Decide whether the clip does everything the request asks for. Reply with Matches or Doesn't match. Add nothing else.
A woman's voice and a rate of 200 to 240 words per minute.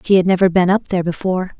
Doesn't match